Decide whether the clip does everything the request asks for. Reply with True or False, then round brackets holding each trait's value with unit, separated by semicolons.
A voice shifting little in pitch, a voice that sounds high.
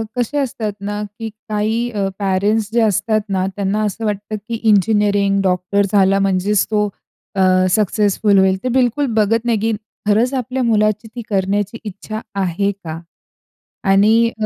True (2.2 semitones; 210 Hz)